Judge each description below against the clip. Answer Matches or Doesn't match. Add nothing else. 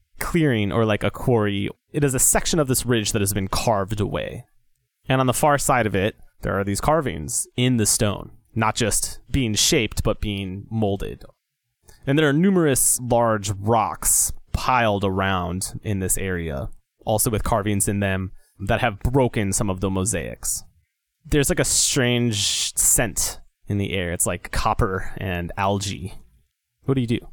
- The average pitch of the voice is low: Matches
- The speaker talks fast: Doesn't match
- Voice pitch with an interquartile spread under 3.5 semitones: Doesn't match